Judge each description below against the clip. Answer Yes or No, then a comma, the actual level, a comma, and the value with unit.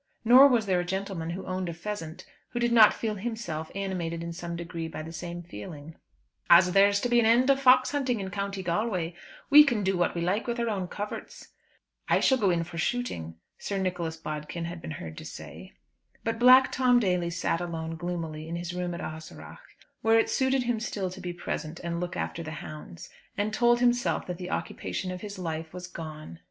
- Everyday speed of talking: No, fast, 215 wpm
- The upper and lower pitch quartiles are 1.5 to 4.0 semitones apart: No, average, 4.9 semitones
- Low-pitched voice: No, medium, 180 Hz